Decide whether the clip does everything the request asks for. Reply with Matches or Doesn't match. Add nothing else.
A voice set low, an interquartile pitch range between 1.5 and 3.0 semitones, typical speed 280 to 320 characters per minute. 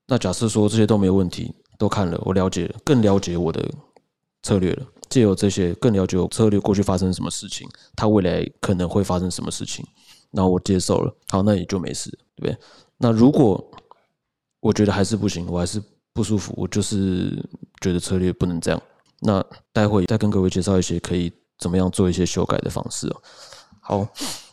Matches